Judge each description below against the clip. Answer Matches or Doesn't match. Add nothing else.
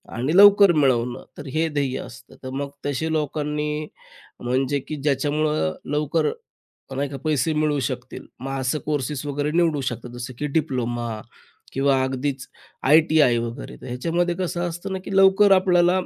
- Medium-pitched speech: Matches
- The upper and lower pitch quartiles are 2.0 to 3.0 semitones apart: Doesn't match